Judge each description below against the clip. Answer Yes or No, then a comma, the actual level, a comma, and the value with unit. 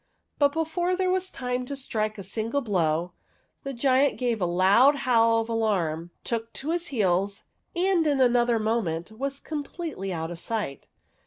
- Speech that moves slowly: No, average, 165 wpm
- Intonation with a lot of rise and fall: Yes, wide, 6.2 semitones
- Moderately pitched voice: No, high, 235 Hz